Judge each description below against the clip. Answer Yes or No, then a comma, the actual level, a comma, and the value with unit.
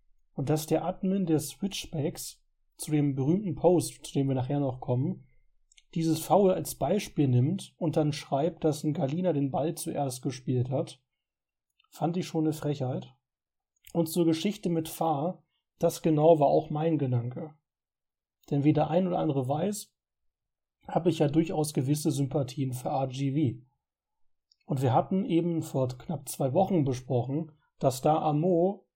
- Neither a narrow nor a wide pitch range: Yes, average, 3.4 semitones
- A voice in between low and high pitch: Yes, medium, 155 Hz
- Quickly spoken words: No, average, 160 wpm